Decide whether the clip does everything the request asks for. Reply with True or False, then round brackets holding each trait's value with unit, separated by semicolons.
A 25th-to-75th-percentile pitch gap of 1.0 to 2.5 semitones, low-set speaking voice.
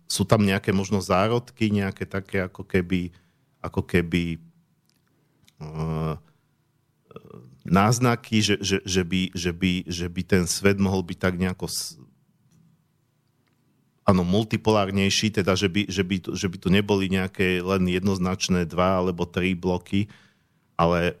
False (2.9 semitones; 95 Hz)